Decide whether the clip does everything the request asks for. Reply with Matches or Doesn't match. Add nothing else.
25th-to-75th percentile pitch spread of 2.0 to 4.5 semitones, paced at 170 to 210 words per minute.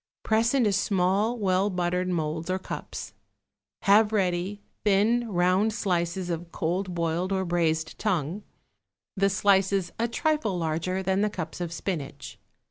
Doesn't match